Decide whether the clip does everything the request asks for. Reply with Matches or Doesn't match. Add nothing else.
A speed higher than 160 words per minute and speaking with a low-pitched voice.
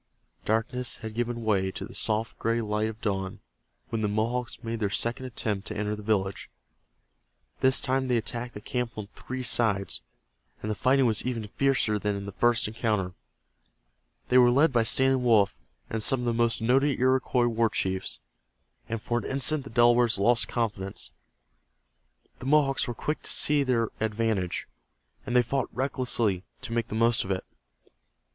Matches